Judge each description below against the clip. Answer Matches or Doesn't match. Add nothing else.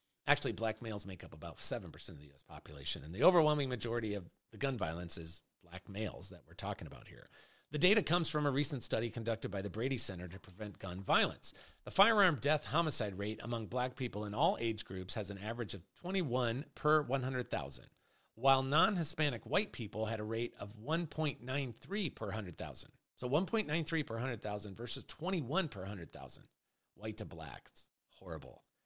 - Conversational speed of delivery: Matches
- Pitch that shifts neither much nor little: Doesn't match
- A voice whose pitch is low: Matches